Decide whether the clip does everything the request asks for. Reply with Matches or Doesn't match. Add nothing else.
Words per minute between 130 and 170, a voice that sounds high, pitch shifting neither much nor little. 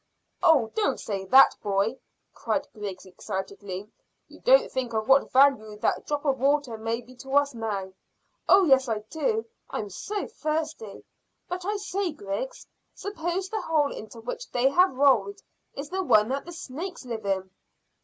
Doesn't match